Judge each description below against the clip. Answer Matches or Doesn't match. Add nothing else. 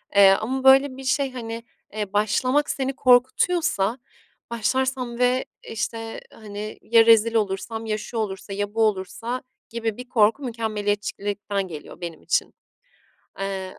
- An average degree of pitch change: Matches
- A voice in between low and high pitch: Doesn't match